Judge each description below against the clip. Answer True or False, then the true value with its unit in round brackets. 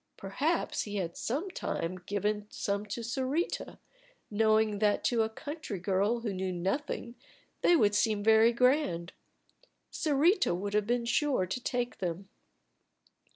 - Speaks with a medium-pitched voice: False (220 Hz)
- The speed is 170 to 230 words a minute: False (145 wpm)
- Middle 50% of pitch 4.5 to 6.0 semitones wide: False (4.0 semitones)